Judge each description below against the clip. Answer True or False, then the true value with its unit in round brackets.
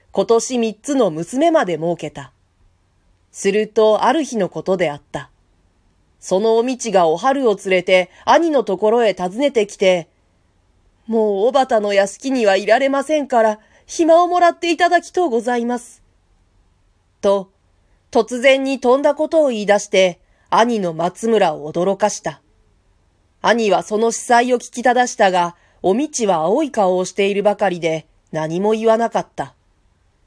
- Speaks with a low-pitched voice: False (200 Hz)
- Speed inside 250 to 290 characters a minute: True (285 characters per minute)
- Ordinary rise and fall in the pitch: False (7.5 semitones)